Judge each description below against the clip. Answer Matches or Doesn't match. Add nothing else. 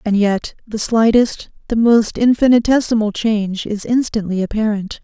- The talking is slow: Matches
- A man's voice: Doesn't match